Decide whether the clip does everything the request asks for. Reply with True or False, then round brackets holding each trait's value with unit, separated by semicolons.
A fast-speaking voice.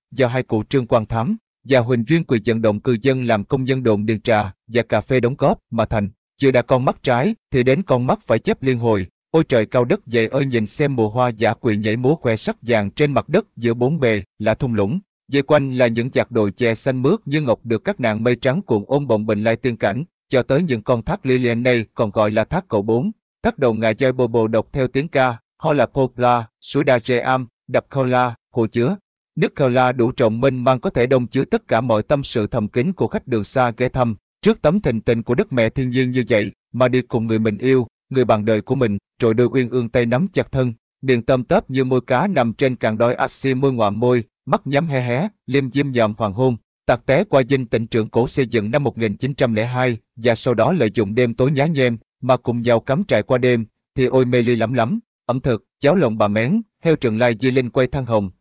True (255 wpm)